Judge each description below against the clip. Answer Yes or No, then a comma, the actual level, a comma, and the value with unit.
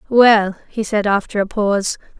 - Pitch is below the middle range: No, high, 210 Hz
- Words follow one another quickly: No, average, 165 wpm